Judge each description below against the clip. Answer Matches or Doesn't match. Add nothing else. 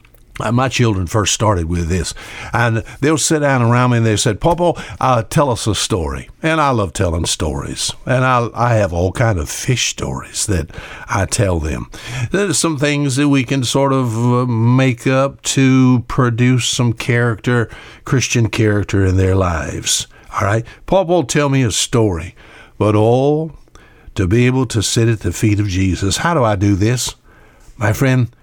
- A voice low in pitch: Matches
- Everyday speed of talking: Matches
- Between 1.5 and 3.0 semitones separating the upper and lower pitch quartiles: Doesn't match